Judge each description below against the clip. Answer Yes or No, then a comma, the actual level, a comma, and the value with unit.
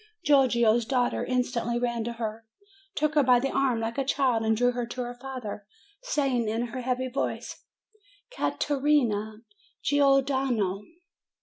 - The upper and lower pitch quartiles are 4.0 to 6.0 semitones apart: No, average, 2.9 semitones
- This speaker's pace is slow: No, average, 160 wpm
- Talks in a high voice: Yes, high, 245 Hz